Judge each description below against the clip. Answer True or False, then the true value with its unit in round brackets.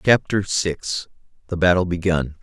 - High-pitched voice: False (90 Hz)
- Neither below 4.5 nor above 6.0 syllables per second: False (4.3 syllables/s)